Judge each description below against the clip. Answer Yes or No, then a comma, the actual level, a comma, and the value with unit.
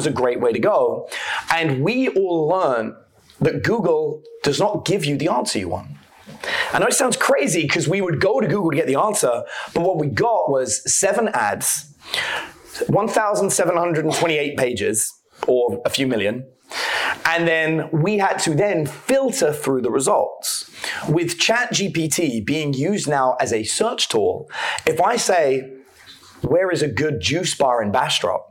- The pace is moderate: Yes, average, 175 wpm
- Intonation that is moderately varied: No, wide, 6.7 semitones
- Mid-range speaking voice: Yes, medium, 165 Hz